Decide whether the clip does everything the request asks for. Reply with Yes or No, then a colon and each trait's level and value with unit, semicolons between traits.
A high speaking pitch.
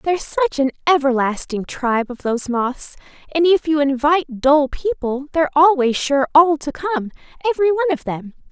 Yes: very high, 295 Hz